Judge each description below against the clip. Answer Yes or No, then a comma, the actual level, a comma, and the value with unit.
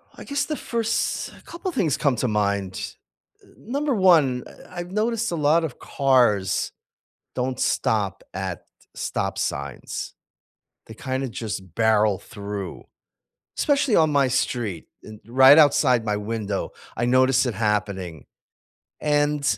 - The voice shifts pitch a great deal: Yes, wide, 7.0 semitones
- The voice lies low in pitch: Yes, low, 125 Hz